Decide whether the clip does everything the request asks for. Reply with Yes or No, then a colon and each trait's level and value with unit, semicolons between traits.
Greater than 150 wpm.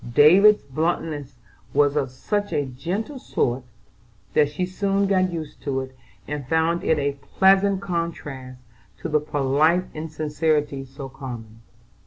No: slow, 135 wpm